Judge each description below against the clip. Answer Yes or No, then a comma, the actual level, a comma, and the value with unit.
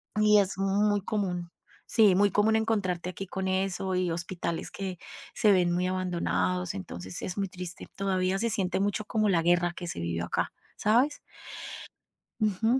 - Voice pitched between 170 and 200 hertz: Yes, medium, 185 Hz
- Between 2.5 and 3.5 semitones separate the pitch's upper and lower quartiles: Yes, average, 2.8 semitones